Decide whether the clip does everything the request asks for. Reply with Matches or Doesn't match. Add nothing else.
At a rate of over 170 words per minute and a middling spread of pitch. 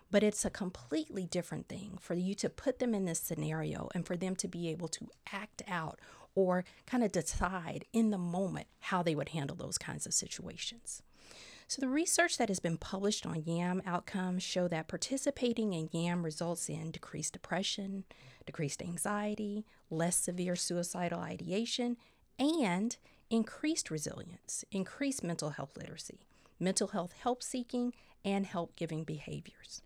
Doesn't match